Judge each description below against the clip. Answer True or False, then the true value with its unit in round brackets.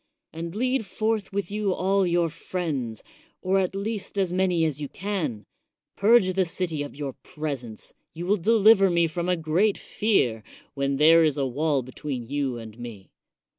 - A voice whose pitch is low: False (170 Hz)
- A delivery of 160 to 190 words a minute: True (170 wpm)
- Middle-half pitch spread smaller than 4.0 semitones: False (5.6 semitones)